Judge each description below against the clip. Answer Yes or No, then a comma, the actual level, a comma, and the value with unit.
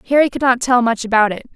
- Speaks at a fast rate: Yes, fast, 270 wpm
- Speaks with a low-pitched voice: No, high, 240 Hz